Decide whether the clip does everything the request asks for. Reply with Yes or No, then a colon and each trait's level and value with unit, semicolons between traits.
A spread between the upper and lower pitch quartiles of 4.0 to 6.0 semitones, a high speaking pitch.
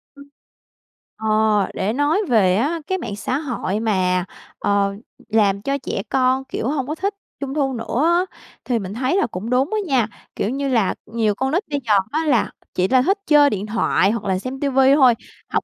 Yes: average, 5.3 semitones; very high, 250 Hz